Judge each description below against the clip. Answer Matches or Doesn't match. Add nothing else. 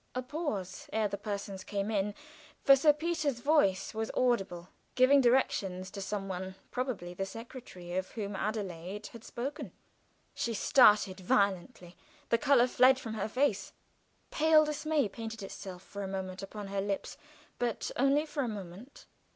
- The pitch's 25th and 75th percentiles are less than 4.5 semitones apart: Doesn't match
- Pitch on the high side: Matches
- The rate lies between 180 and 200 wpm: Doesn't match